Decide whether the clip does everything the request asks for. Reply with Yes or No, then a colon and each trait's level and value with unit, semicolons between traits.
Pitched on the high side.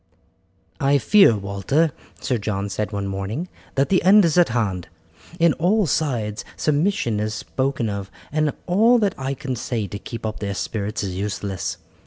No: low, 120 Hz